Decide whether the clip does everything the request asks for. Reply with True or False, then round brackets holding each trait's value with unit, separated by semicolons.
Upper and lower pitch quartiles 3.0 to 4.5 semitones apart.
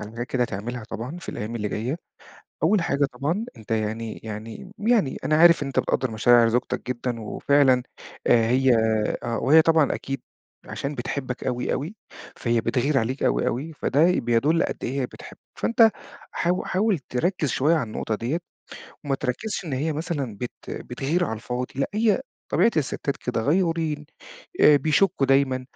False (4.9 semitones)